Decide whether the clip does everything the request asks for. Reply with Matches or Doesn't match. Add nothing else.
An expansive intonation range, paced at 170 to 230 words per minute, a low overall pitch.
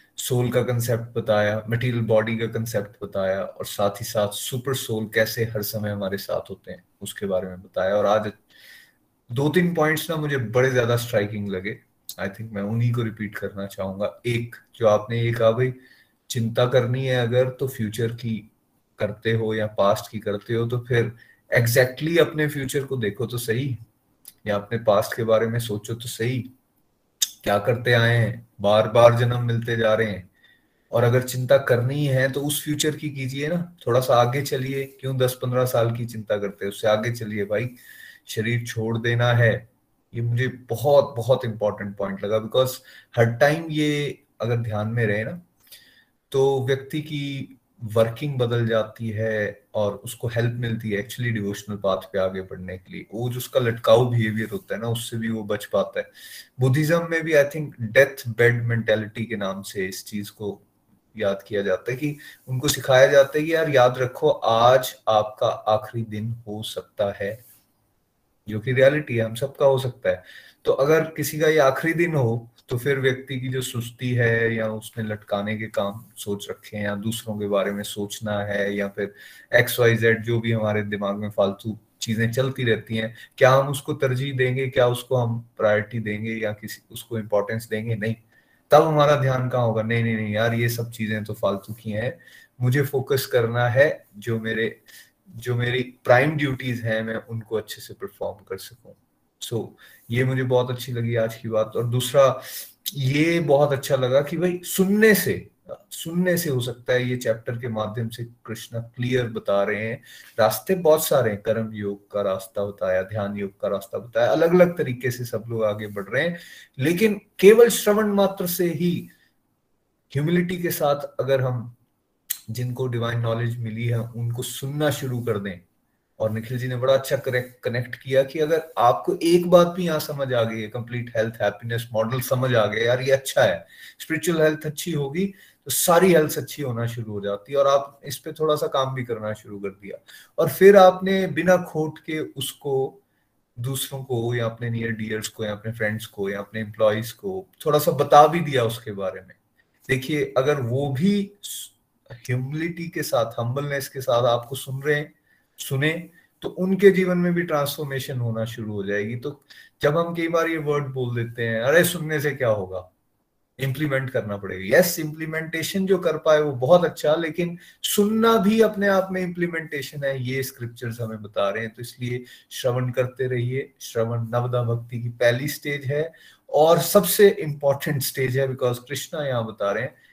Doesn't match